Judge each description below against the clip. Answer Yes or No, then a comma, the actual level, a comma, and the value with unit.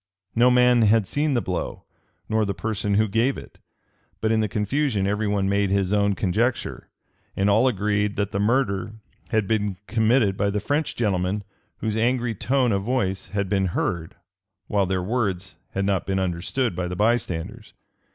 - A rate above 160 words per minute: Yes, average, 175 wpm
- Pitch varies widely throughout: No, average, 2.9 semitones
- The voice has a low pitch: Yes, low, 105 Hz